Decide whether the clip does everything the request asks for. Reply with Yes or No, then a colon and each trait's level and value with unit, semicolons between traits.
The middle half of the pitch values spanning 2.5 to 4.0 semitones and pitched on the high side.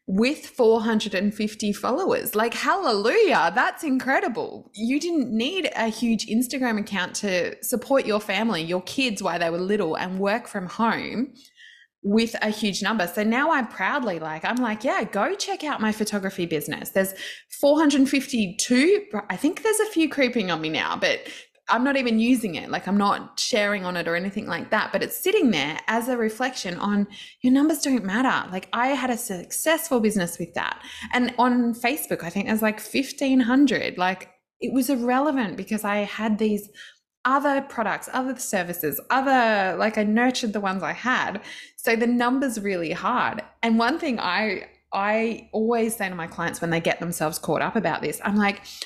No: average, 4.4 semitones; high, 225 Hz